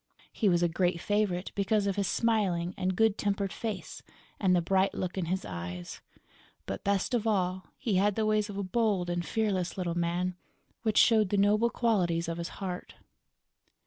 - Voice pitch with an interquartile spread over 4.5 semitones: No, average, 3.0 semitones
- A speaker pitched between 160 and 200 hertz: Yes, high, 190 Hz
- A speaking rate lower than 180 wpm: No, average, 185 wpm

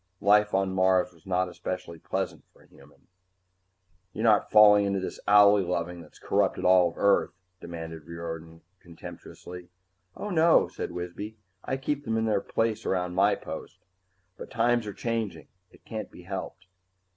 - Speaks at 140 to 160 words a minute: Yes, average, 155 wpm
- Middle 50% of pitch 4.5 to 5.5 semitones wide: No, average, 3.5 semitones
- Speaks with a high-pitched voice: No, very low, 95 Hz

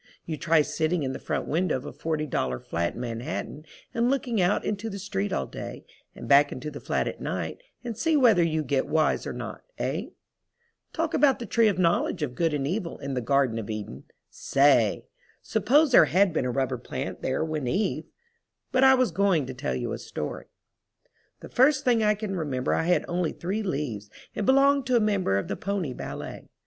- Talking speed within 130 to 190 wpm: No, average, 200 wpm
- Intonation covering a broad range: Yes, wide, 8.4 semitones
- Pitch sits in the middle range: Yes, medium, 170 Hz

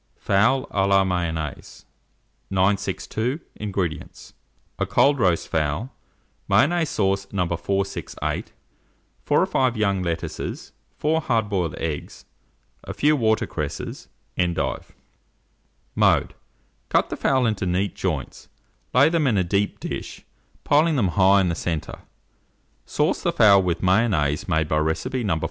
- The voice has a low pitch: Yes, low, 100 Hz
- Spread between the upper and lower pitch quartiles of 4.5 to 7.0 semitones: Yes, average, 4.9 semitones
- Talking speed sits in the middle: No, slow, 130 wpm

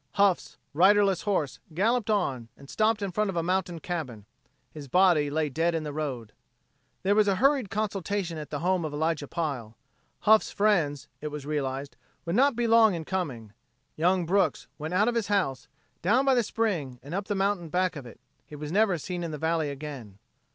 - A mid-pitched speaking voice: Yes, medium, 175 Hz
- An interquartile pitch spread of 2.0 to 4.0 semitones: No, wide, 5.4 semitones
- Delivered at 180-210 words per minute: Yes, average, 200 wpm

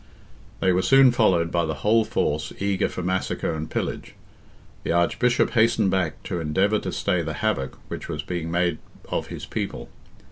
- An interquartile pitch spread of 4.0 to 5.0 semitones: Yes, average, 4.3 semitones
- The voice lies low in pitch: Yes, very low, 90 Hz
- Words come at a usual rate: Yes, average, 175 wpm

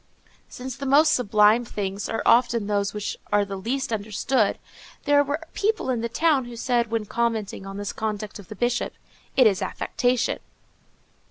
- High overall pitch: Yes, high, 230 Hz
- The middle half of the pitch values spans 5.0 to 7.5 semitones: No, average, 3.6 semitones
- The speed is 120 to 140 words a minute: No, average, 175 wpm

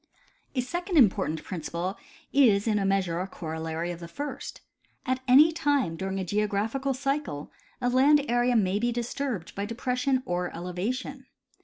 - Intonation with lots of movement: Yes, wide, 6.4 semitones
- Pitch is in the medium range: No, high, 220 Hz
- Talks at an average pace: Yes, average, 155 wpm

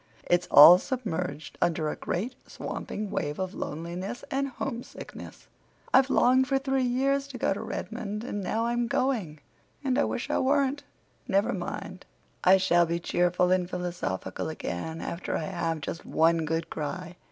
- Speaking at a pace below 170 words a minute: Yes, average, 150 wpm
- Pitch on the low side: No, medium, 185 Hz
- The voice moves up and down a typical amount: No, wide, 6.7 semitones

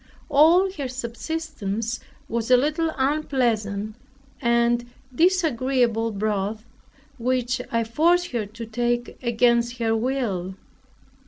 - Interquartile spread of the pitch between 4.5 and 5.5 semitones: No, average, 3.4 semitones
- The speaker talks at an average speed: No, slow, 100 wpm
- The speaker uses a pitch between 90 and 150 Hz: No, high, 240 Hz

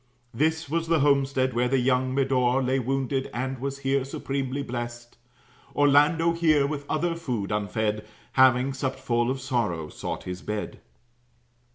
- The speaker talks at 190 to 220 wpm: No, average, 150 wpm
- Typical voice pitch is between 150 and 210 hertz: No, low, 135 Hz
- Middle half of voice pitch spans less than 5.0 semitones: Yes, narrow, 2.5 semitones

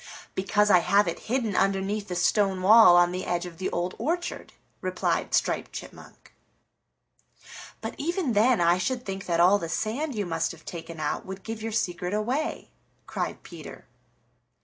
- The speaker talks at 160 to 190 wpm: Yes, average, 170 wpm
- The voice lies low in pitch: No, high, 195 Hz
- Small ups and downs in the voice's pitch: No, average, 4.1 semitones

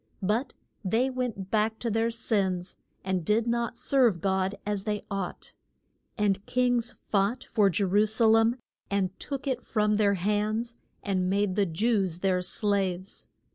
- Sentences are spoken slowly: No, average, 155 wpm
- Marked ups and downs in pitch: No, average, 3.1 semitones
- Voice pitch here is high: Yes, high, 210 Hz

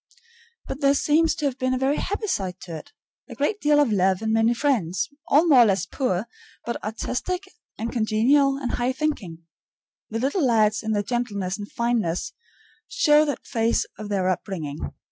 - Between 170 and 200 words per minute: Yes, average, 185 wpm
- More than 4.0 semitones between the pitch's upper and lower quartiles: Yes, wide, 5.6 semitones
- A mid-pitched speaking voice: No, high, 235 Hz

